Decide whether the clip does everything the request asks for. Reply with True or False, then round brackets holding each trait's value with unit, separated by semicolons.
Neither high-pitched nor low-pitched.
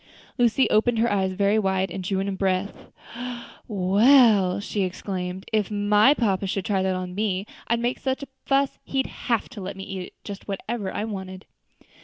False (200 Hz)